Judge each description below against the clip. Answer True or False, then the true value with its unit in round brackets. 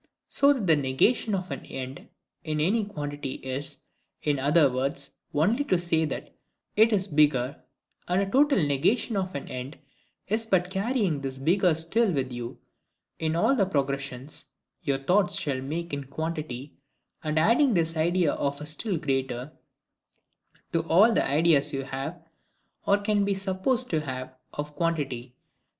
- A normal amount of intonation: False (5.8 semitones)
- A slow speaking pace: False (155 wpm)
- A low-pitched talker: False (160 Hz)